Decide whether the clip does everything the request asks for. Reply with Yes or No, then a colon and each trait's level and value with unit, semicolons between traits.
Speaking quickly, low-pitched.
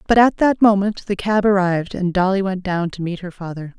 No: fast, 240 wpm; high, 190 Hz